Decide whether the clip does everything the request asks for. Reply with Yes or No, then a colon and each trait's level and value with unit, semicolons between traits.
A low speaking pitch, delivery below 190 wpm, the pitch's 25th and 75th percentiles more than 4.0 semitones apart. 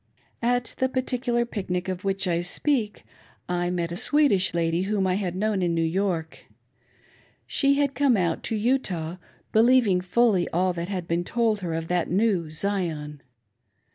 No: high, 190 Hz; average, 170 wpm; average, 5.1 semitones